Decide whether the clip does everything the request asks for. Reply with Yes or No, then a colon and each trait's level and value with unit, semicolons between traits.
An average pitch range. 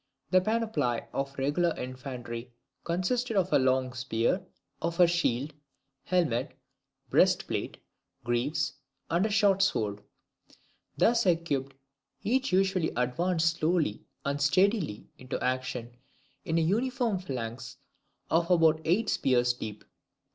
No: wide, 6.4 semitones